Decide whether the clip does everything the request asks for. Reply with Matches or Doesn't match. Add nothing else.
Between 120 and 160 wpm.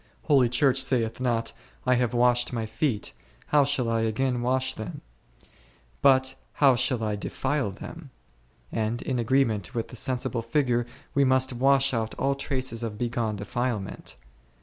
Matches